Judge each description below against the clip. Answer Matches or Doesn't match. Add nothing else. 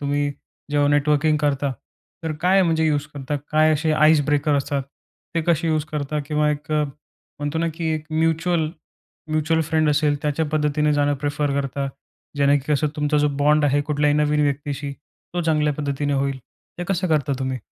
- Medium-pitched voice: Matches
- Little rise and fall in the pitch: Matches